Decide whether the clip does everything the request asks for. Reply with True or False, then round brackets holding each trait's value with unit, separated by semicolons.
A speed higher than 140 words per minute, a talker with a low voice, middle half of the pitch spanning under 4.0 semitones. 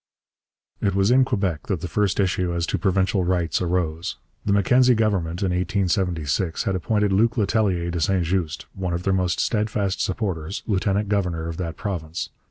True (175 wpm; 95 Hz; 2.9 semitones)